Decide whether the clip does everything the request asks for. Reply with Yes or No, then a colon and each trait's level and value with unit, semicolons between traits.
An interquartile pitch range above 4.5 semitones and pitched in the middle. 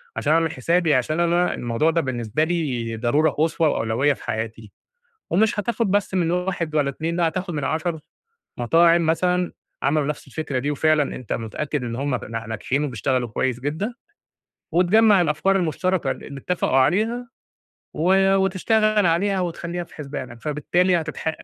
Yes: average, 4.9 semitones; medium, 160 Hz